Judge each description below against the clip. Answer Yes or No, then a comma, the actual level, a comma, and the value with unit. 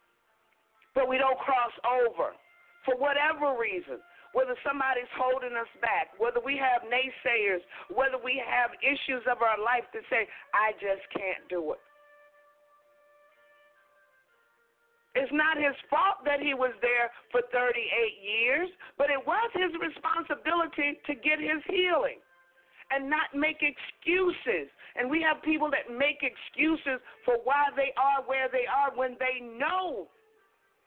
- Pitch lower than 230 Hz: No, very high, 280 Hz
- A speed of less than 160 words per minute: Yes, average, 140 wpm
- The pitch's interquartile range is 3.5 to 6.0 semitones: Yes, average, 4.1 semitones